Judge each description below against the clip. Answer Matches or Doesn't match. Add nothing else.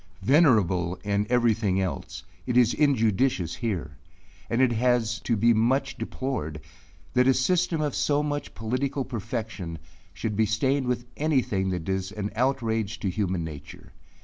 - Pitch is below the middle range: Matches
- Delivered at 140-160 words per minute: Matches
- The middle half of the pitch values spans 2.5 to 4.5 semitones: Doesn't match